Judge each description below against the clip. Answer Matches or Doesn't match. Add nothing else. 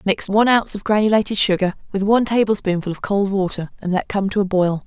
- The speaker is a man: Doesn't match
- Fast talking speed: Matches